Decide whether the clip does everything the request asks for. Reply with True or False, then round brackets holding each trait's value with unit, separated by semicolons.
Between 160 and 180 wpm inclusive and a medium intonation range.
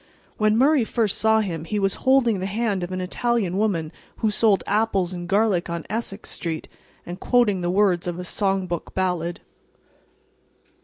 True (170 wpm; 3.8 semitones)